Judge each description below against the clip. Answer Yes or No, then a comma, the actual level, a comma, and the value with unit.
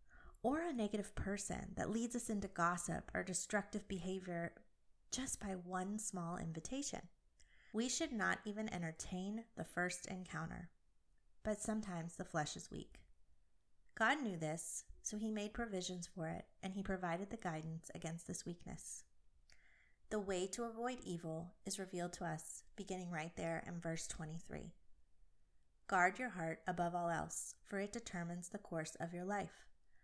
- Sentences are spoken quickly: No, average, 155 wpm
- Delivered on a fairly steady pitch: No, average, 4.2 semitones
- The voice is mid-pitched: Yes, medium, 180 Hz